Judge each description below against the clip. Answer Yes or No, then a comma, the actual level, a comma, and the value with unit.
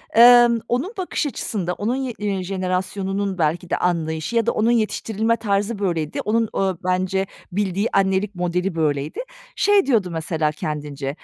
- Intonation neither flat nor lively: Yes, average, 4.4 semitones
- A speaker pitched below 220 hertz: Yes, high, 195 Hz